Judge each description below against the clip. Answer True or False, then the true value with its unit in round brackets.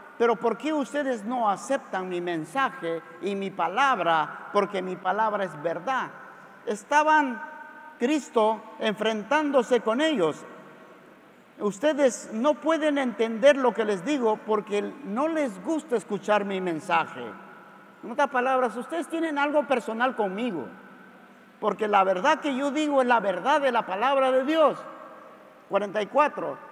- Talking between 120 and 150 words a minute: True (135 wpm)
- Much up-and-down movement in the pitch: True (5.8 semitones)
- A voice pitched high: True (245 Hz)